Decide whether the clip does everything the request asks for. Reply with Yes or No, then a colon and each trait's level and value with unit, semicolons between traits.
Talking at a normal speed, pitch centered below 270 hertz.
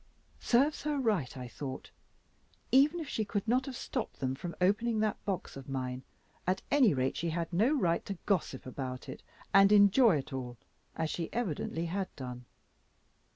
Yes: average, 175 wpm; medium, 185 Hz